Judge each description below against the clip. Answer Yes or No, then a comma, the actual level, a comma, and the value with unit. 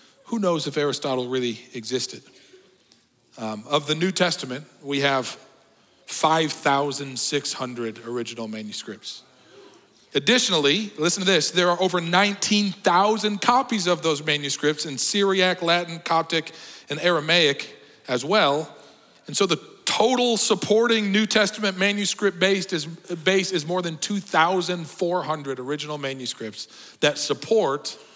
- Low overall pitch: No, medium, 165 Hz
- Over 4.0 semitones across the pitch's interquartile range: Yes, average, 5.3 semitones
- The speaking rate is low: Yes, slow, 115 wpm